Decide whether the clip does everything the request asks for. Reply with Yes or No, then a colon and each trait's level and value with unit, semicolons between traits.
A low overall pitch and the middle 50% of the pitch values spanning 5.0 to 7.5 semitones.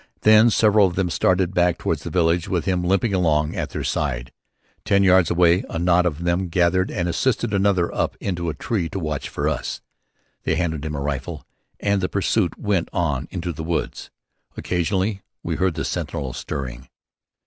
No: very low, 90 Hz; average, 3.2 semitones